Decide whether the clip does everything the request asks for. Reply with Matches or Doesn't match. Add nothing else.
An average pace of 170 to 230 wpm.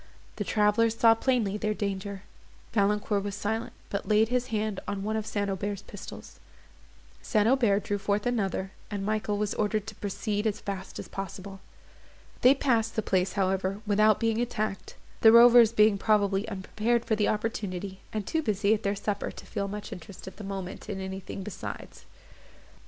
Matches